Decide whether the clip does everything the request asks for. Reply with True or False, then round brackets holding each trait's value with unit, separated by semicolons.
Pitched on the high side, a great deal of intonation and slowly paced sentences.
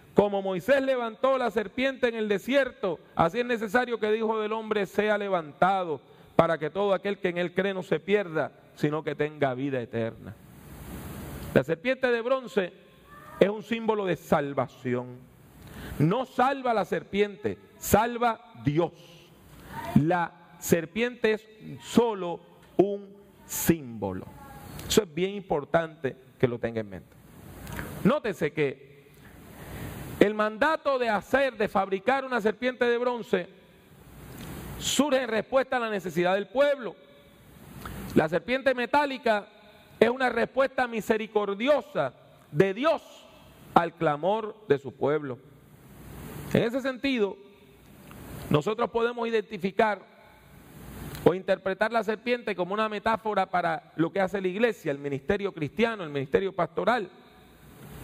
True (200 Hz; 5.9 semitones; 130 wpm)